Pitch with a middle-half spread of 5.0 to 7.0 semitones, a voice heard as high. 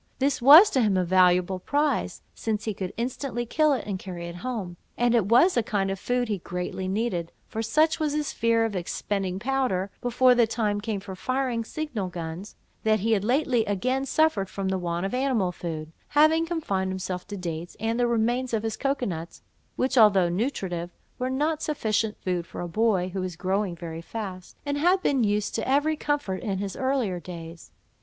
Yes: wide, 5.6 semitones; high, 215 Hz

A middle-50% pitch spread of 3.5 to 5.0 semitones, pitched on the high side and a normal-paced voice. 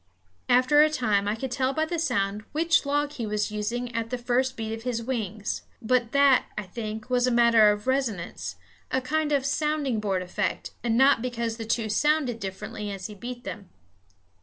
Yes: average, 3.8 semitones; high, 240 Hz; average, 195 wpm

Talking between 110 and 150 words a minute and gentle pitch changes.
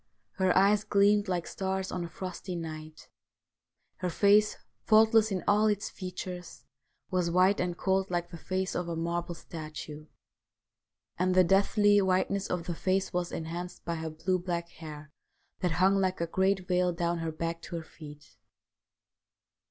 No: average, 160 wpm; narrow, 2.2 semitones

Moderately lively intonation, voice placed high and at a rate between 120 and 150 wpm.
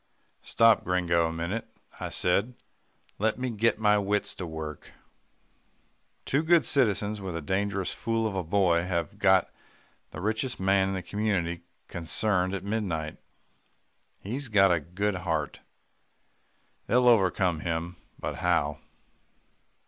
No: average, 4.0 semitones; very low, 95 Hz; slow, 135 wpm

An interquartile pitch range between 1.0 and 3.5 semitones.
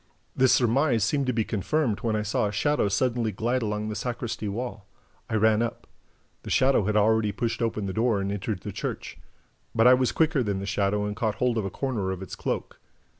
Yes: average, 3.1 semitones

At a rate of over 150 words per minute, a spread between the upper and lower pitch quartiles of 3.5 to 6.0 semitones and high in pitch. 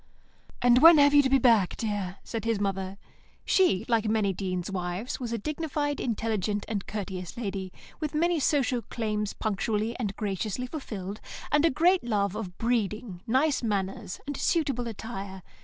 Yes: average, 160 wpm; average, 4.7 semitones; high, 220 Hz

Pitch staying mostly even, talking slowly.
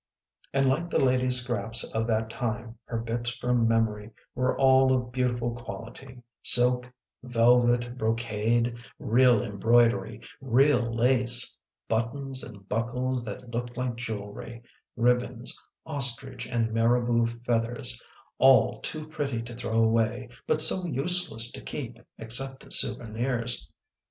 Yes: narrow, 1.8 semitones; slow, 125 wpm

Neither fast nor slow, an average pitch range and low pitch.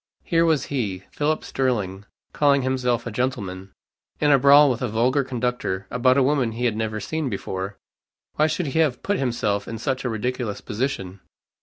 Yes: average, 180 wpm; average, 4.5 semitones; low, 125 Hz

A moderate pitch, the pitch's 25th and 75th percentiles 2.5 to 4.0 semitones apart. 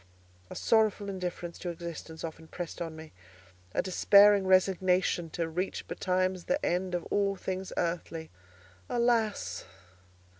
Yes: medium, 180 Hz; average, 2.8 semitones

